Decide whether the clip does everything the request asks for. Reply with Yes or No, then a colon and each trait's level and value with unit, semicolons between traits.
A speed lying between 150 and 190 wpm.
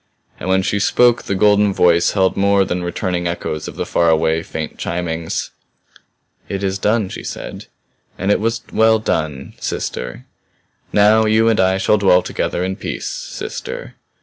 Yes: average, 165 wpm